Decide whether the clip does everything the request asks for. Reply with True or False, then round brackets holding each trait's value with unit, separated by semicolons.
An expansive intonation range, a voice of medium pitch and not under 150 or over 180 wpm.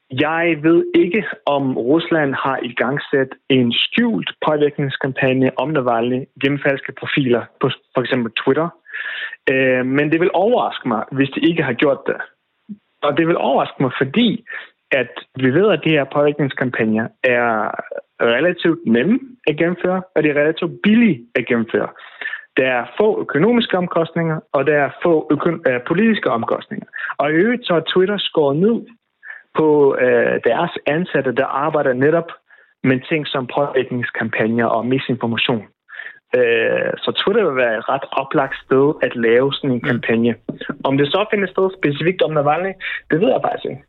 True (6.3 semitones; 150 Hz; 165 wpm)